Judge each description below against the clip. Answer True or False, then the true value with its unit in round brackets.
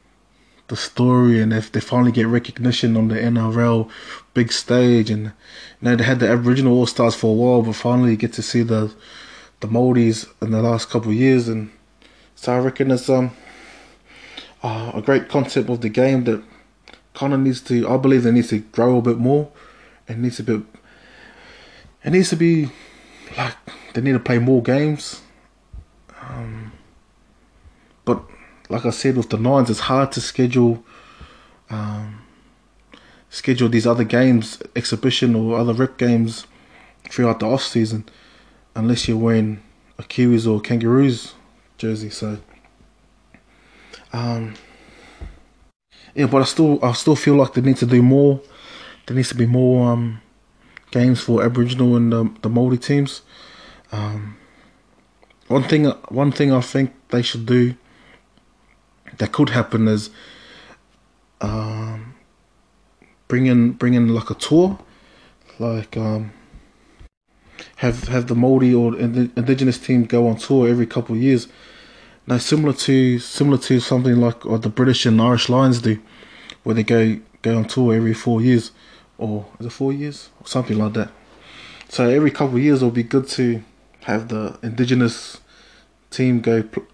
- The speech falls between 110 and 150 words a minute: False (160 wpm)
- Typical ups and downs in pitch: False (2.1 semitones)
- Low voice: True (120 Hz)